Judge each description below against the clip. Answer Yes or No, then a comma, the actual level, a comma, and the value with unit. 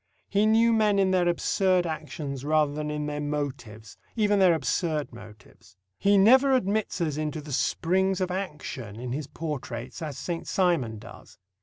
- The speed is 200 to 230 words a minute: No, average, 165 wpm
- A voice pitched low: No, medium, 155 Hz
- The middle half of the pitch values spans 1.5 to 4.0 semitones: No, average, 5.0 semitones